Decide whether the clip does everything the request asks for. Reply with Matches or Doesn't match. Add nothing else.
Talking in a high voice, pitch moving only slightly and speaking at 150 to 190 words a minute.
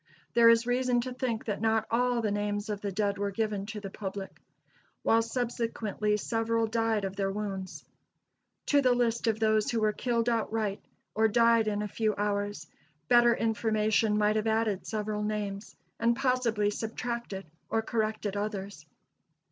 Matches